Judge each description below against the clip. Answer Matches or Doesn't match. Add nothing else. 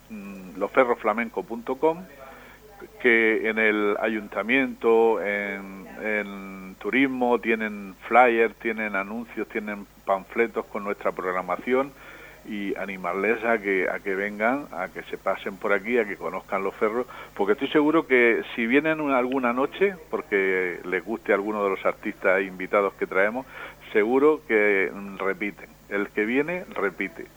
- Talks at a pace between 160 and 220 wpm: Doesn't match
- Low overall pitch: Matches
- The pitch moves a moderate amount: Matches